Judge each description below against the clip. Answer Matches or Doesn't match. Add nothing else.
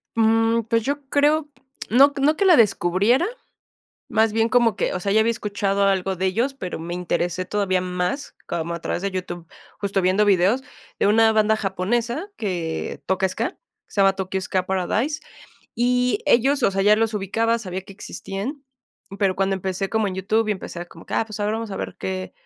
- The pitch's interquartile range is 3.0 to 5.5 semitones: Matches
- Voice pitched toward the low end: Doesn't match